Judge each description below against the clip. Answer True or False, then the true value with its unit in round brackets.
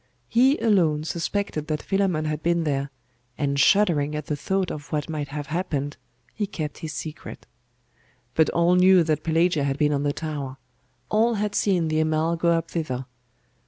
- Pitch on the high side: False (155 Hz)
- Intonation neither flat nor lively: True (3.3 semitones)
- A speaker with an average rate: True (175 wpm)